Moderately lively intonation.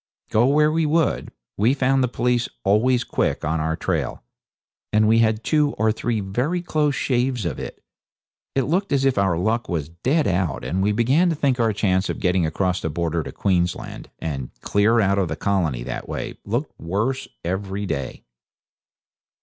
No: wide, 6.4 semitones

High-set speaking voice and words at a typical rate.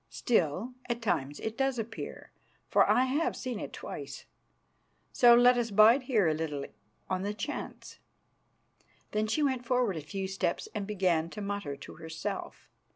Yes: high, 210 Hz; average, 160 wpm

